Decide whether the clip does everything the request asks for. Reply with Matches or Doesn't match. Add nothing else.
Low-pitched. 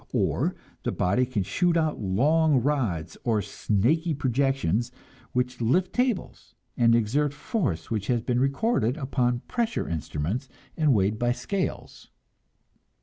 Matches